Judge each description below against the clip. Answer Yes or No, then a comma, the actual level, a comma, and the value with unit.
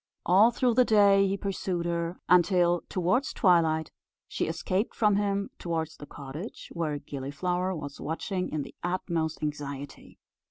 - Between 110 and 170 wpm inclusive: Yes, average, 145 wpm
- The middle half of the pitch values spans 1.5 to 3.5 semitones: No, average, 3.9 semitones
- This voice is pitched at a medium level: Yes, medium, 175 Hz